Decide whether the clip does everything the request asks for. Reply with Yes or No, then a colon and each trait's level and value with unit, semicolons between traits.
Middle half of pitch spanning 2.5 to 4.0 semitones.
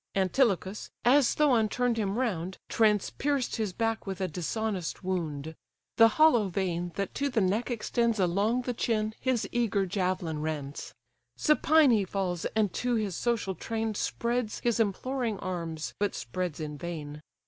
No: average, 4.6 semitones